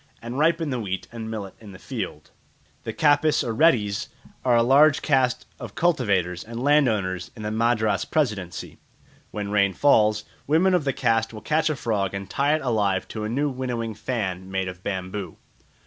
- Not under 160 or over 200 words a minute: Yes, average, 180 wpm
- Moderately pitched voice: No, low, 115 Hz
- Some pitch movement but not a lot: No, wide, 5.7 semitones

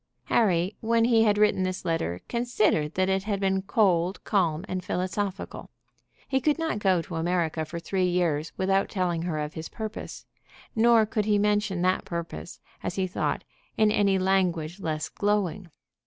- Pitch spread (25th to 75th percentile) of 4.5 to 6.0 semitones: No, average, 3.5 semitones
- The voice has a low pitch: No, high, 190 Hz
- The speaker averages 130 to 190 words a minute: Yes, average, 170 wpm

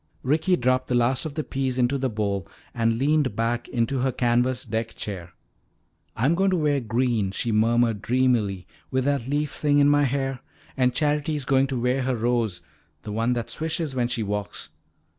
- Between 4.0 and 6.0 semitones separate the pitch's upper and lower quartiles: No, average, 3.4 semitones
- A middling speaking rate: Yes, average, 185 wpm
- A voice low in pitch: Yes, low, 125 Hz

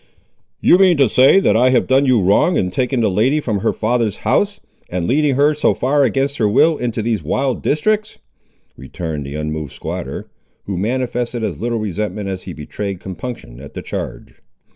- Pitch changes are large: Yes, wide, 5.9 semitones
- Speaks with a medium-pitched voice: No, low, 115 Hz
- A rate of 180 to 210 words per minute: Yes, average, 185 wpm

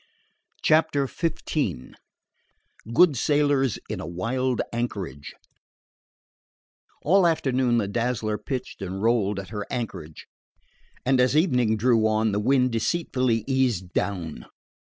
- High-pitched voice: No, low, 120 Hz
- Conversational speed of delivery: No, slow, 110 wpm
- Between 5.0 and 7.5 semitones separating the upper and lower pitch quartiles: No, average, 4.4 semitones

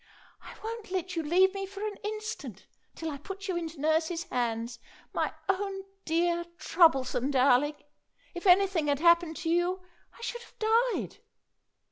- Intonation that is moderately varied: Yes, average, 4.4 semitones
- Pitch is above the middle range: Yes, very high, 345 Hz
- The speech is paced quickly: No, average, 155 wpm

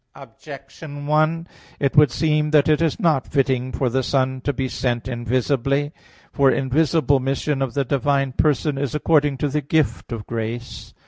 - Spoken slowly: No, average, 170 wpm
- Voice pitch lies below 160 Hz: Yes, medium, 140 Hz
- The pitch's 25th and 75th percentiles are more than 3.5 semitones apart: No, narrow, 2.6 semitones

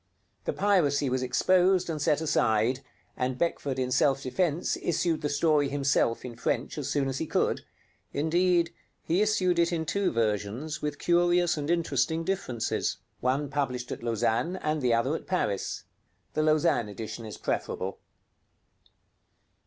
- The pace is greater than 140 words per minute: Yes, average, 150 wpm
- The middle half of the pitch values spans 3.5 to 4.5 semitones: No, average, 5.2 semitones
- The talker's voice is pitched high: No, medium, 145 Hz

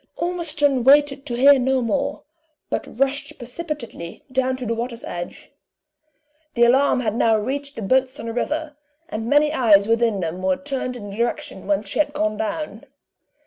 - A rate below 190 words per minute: Yes, average, 175 wpm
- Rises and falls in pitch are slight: No, average, 4.2 semitones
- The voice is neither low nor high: No, very high, 255 Hz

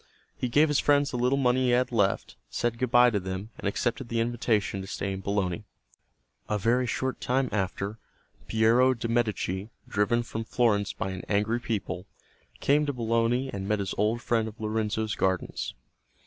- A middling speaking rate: Yes, average, 180 wpm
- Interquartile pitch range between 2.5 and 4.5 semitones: Yes, average, 3.2 semitones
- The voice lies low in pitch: Yes, low, 115 Hz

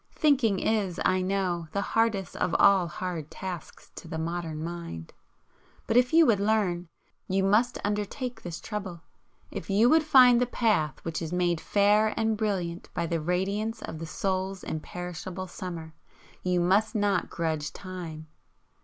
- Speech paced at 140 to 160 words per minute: Yes, average, 155 wpm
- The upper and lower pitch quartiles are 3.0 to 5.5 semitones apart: Yes, average, 3.9 semitones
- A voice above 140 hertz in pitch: Yes, medium, 185 Hz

